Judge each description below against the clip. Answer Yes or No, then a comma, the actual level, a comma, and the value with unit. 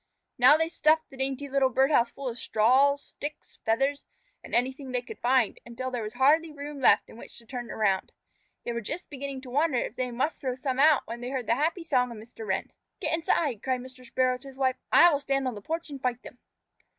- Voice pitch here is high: Yes, very high, 260 Hz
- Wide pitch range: No, narrow, 2.6 semitones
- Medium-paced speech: No, fast, 235 wpm